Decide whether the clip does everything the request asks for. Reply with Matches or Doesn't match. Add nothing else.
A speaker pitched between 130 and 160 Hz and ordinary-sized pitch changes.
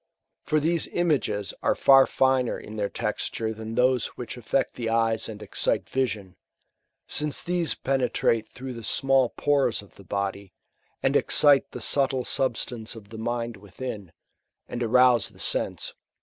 Doesn't match